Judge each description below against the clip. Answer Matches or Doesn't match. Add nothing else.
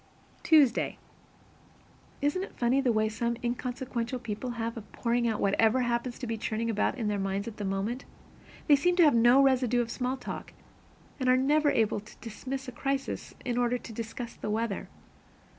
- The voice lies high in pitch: Matches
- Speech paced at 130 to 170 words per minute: Doesn't match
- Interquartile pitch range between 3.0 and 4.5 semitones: Doesn't match